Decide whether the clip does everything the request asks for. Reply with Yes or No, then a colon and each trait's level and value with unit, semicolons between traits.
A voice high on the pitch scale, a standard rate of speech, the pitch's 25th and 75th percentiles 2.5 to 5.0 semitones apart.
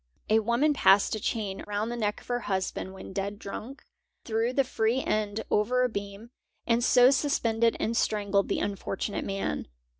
Yes: high, 220 Hz; average, 175 wpm; average, 3.0 semitones